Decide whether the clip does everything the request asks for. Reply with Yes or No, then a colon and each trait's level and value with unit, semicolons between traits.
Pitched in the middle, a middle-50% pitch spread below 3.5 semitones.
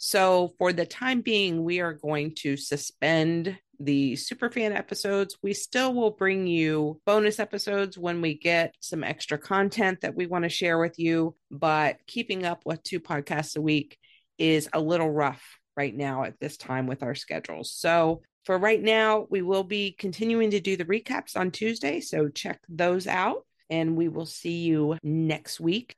No: medium, 170 Hz; average, 4.3 semitones